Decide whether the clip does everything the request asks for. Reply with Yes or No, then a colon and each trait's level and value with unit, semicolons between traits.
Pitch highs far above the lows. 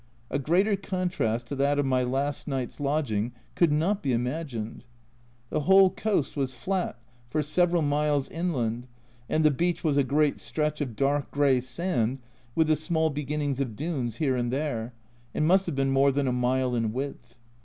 No: average, 3.7 semitones